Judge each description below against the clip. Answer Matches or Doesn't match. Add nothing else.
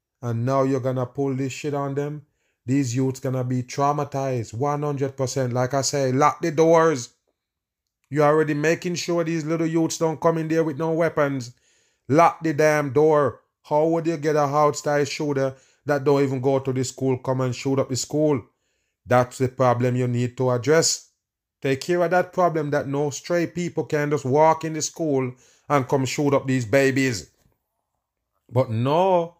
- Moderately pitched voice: Matches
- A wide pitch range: Doesn't match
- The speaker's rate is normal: Matches